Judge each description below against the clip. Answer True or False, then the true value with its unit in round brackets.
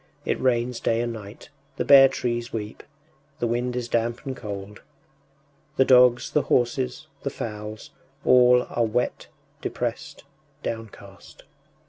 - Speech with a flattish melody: True (1.9 semitones)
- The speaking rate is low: True (130 wpm)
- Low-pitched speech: True (120 Hz)